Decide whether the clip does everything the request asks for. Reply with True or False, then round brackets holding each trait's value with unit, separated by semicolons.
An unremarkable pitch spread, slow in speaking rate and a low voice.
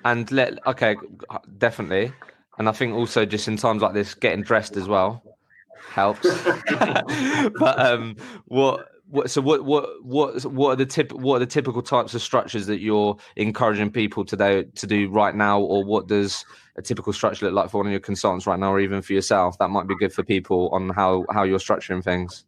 False (3.1 semitones; 205 wpm; 105 Hz)